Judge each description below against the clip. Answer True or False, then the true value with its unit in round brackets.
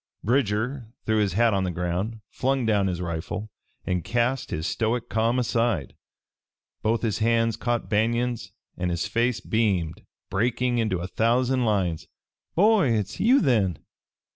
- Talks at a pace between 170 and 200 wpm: False (145 wpm)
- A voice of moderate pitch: False (110 Hz)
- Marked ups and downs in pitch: False (3.9 semitones)